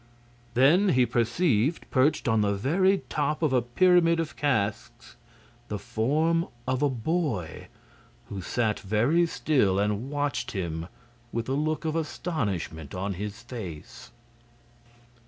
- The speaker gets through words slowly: Yes, slow, 130 wpm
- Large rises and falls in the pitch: Yes, wide, 7.1 semitones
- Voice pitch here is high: No, low, 125 Hz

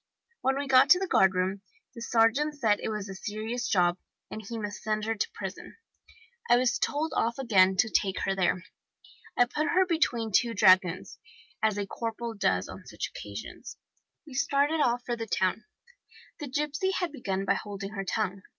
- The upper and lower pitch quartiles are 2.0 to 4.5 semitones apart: No, average, 5.1 semitones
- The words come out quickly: No, average, 185 wpm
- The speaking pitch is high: Yes, high, 225 Hz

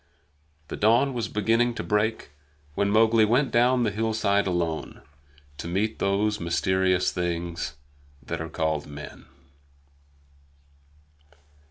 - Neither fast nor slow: No, slow, 115 wpm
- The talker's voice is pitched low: Yes, low, 100 Hz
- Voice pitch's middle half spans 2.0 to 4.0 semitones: No, average, 4.5 semitones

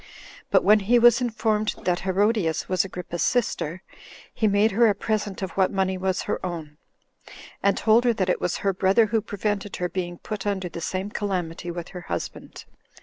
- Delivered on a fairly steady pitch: No, average, 3.0 semitones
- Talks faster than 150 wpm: Yes, average, 190 wpm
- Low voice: No, high, 195 Hz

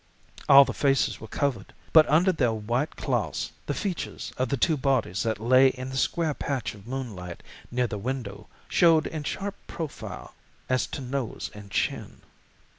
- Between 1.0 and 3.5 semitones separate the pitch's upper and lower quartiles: No, average, 4.2 semitones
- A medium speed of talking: Yes, average, 170 wpm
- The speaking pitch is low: Yes, low, 130 Hz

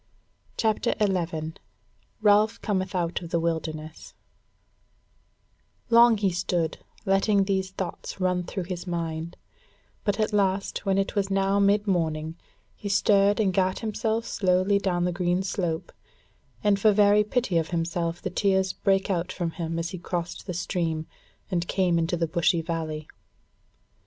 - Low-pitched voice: No, medium, 185 Hz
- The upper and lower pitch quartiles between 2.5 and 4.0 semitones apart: Yes, average, 2.9 semitones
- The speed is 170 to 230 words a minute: No, average, 145 wpm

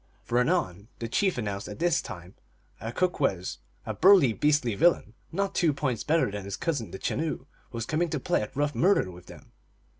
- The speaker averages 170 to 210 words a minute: Yes, average, 190 wpm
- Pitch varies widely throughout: Yes, wide, 7.6 semitones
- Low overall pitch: Yes, low, 130 Hz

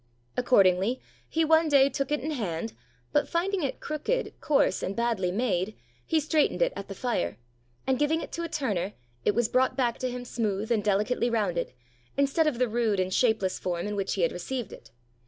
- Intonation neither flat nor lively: No, wide, 6.4 semitones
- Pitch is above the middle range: Yes, high, 240 Hz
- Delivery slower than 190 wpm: No, average, 200 wpm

